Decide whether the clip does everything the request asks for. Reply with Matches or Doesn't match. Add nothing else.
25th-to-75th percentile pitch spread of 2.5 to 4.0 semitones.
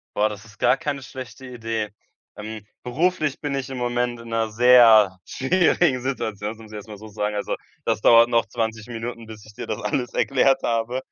Matches